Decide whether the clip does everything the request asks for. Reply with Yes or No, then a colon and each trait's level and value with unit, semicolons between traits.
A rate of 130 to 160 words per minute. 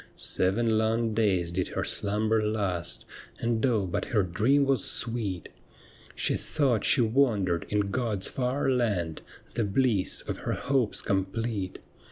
Yes: average, 140 wpm